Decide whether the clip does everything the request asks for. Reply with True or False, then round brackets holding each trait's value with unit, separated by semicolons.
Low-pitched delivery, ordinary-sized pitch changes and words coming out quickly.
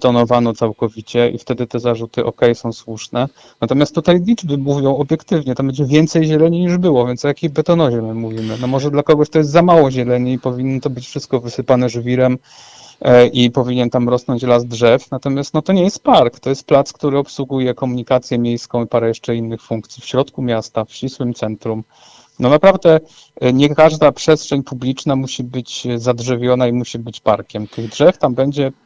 True (130 Hz; 3.3 semitones; 185 wpm)